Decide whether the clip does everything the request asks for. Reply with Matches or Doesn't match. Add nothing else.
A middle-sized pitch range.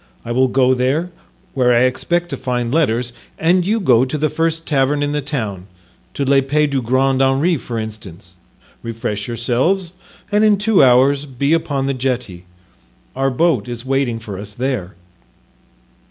Matches